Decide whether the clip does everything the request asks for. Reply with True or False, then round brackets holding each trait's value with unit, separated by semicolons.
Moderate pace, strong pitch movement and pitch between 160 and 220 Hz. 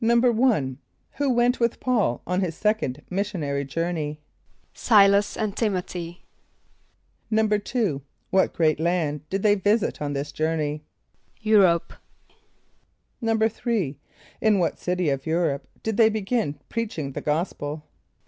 False (120 wpm; 6.3 semitones; 185 Hz)